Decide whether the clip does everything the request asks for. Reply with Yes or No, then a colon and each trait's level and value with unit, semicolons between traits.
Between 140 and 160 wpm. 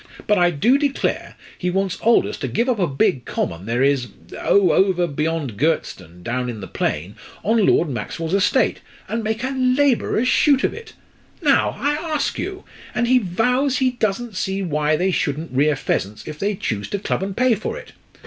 No: average, 190 wpm